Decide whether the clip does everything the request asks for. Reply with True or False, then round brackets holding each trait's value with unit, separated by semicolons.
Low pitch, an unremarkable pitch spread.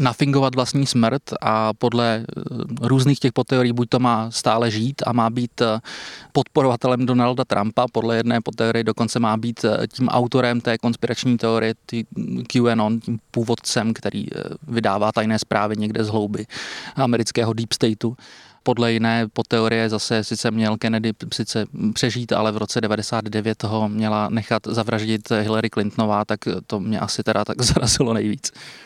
False (115 Hz; 1.9 semitones)